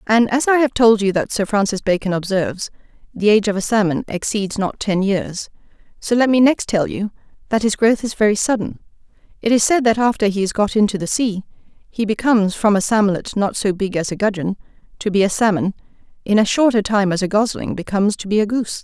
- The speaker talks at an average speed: No, fast, 225 wpm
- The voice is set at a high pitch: Yes, high, 210 Hz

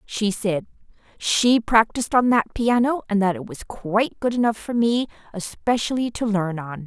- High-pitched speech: Yes, high, 220 Hz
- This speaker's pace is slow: No, average, 175 wpm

